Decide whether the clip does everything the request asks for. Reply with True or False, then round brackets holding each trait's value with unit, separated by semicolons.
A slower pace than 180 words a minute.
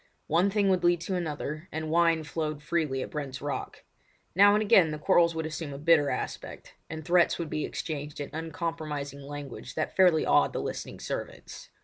False (190 wpm)